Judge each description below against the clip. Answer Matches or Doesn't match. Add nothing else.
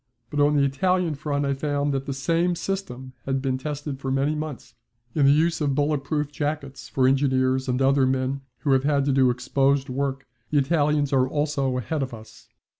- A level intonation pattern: Matches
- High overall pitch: Doesn't match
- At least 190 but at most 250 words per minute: Matches